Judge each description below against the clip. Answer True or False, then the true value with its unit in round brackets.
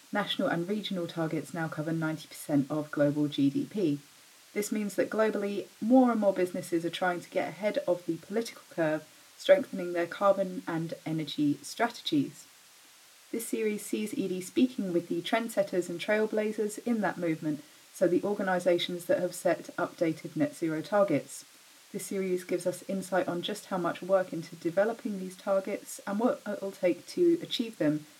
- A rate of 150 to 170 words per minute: True (165 wpm)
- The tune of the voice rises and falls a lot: False (4.3 semitones)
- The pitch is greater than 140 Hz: True (185 Hz)